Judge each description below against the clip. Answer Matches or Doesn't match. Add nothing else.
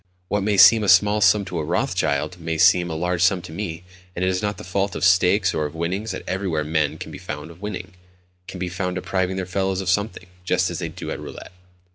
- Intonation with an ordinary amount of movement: Doesn't match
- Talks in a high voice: Doesn't match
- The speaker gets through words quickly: Matches